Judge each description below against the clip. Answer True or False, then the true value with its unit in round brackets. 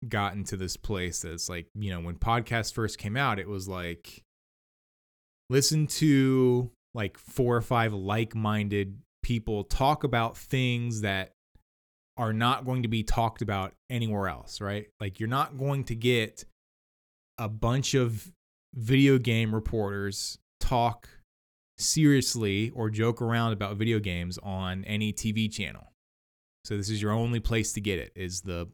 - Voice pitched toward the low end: True (110 Hz)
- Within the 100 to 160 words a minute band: True (155 wpm)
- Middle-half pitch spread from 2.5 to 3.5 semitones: False (3.9 semitones)